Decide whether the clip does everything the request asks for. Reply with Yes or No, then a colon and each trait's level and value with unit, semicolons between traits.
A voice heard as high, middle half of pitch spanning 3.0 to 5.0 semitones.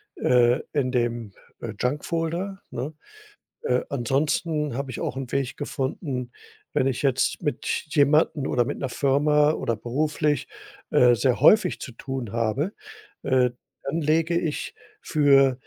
No: low, 135 Hz; average, 3.3 semitones